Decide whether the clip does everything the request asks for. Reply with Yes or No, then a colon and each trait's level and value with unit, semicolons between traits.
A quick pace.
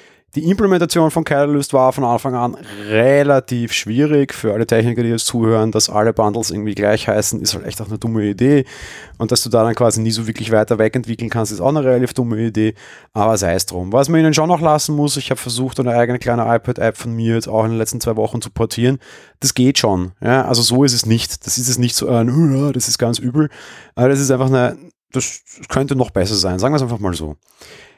Yes: fast, 240 wpm